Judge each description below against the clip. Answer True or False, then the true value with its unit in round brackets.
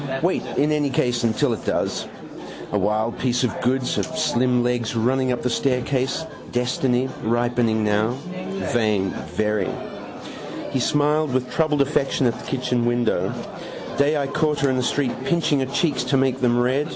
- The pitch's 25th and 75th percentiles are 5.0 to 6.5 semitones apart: False (2.7 semitones)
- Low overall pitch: True (125 Hz)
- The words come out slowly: False (165 wpm)